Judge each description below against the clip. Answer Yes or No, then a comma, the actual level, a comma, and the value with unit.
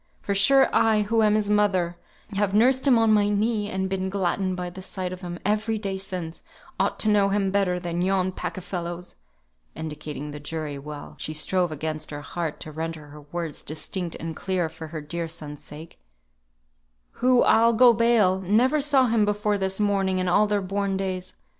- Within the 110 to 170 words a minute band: No, average, 195 wpm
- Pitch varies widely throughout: No, average, 3.8 semitones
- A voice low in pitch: No, high, 190 Hz